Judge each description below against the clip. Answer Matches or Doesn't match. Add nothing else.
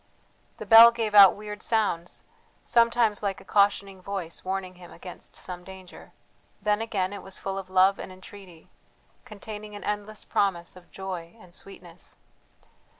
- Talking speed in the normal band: Matches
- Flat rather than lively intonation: Matches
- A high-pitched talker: Matches